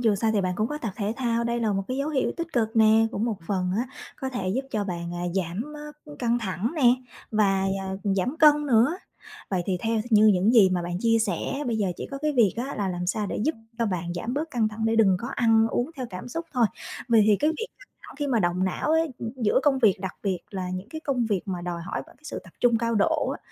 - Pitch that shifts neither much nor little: Yes, average, 4.9 semitones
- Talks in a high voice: Yes, high, 225 Hz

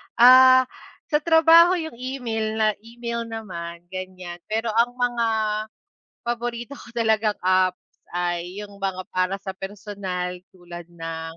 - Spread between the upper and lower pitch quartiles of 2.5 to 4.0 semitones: No, average, 4.6 semitones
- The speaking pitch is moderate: No, high, 215 Hz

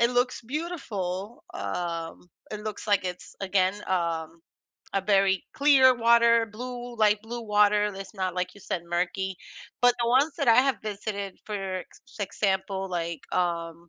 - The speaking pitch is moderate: No, high, 200 Hz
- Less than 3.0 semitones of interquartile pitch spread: No, average, 4.2 semitones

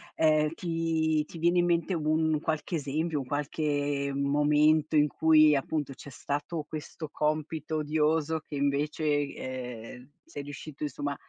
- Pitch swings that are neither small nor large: No, narrow, 1.7 semitones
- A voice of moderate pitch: Yes, medium, 150 Hz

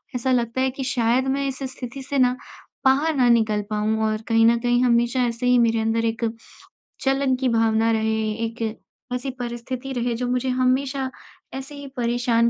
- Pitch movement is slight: Yes, narrow, 2.3 semitones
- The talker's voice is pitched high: Yes, high, 245 Hz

